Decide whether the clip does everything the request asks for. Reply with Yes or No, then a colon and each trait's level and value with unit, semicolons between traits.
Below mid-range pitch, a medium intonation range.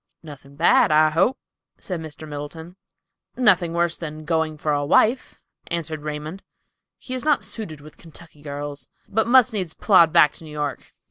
No: medium, 160 Hz; average, 3.9 semitones